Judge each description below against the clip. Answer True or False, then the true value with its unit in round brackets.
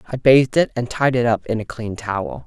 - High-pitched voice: False (115 Hz)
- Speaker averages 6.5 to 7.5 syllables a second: False (5.7 syllables/s)